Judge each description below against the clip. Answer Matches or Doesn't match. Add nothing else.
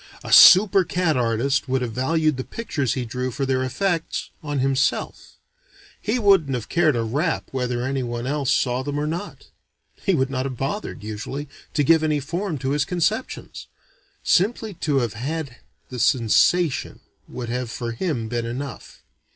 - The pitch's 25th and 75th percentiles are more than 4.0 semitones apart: Matches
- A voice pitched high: Doesn't match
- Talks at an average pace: Matches